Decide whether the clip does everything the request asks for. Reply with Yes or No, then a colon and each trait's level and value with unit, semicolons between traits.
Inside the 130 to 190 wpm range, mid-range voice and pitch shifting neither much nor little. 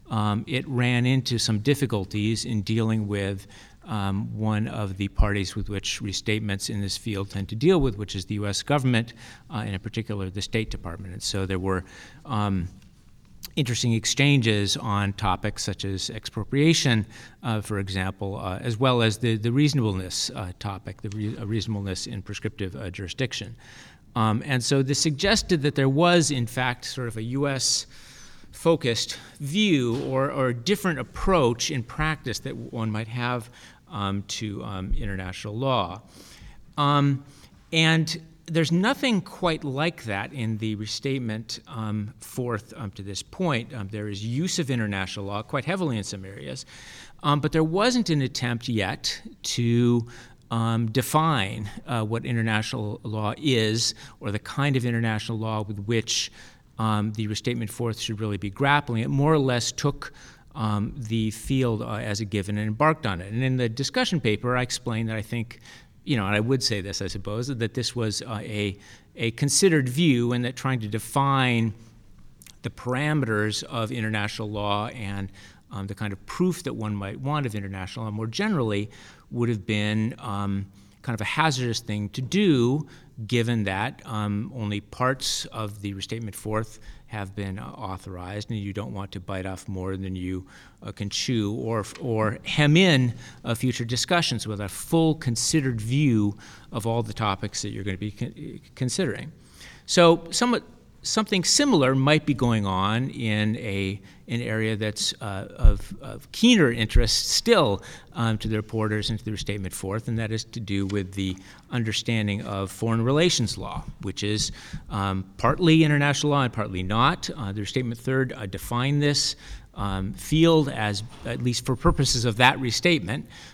No: average, 170 wpm; low, 115 Hz; average, 4.2 semitones